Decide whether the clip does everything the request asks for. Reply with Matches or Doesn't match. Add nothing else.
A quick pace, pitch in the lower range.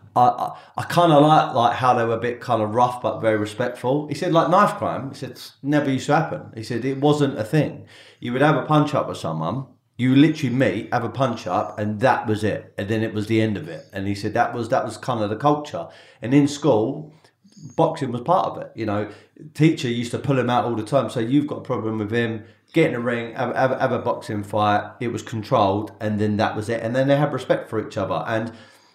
Matches